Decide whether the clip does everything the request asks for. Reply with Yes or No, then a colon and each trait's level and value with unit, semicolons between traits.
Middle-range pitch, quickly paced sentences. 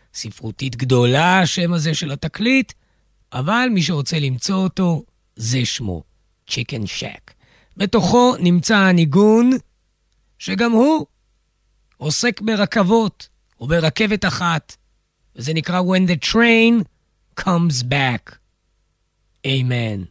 No: medium, 155 Hz; slow, 100 wpm